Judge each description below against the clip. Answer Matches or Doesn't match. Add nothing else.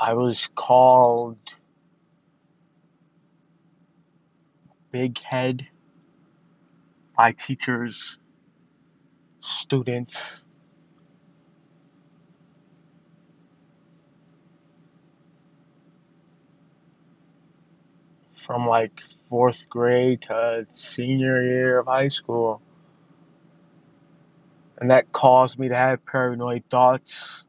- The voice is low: Matches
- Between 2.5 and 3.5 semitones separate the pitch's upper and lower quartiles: Matches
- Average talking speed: Doesn't match